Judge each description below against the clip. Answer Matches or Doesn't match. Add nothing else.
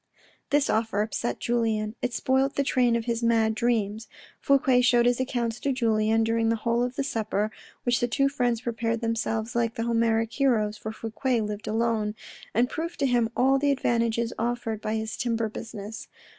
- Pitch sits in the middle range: Doesn't match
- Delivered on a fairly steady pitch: Matches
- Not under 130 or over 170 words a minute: Doesn't match